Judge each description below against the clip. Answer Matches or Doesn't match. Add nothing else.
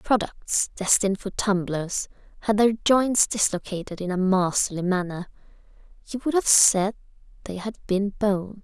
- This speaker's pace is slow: Matches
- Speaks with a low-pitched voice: Doesn't match